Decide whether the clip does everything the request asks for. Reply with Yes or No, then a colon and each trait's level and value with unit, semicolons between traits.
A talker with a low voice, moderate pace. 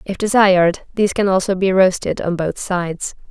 No: high, 190 Hz; average, 180 wpm